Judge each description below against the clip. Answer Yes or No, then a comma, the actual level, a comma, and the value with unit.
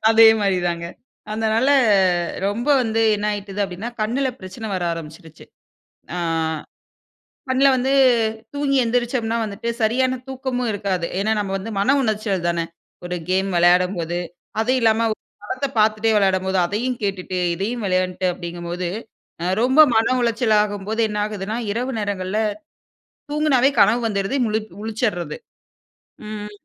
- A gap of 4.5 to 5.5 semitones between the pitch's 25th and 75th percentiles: No, average, 3.7 semitones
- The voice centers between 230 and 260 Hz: No, high, 210 Hz